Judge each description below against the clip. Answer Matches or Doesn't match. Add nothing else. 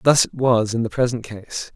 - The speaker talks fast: Matches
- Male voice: Matches